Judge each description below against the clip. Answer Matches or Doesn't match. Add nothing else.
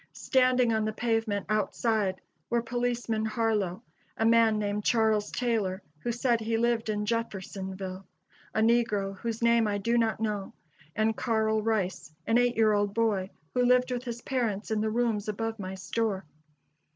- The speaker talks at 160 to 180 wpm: Matches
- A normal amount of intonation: Doesn't match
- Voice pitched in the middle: Doesn't match